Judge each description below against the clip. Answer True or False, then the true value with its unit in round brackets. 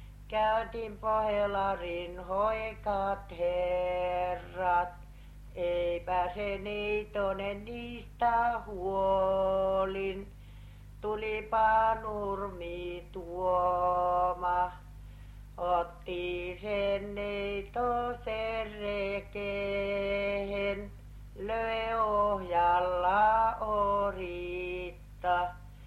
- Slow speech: True (40 wpm)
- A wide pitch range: False (2.8 semitones)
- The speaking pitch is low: False (195 Hz)